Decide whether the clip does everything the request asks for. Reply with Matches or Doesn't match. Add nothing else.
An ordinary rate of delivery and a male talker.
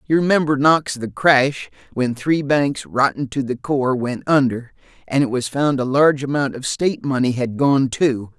Matches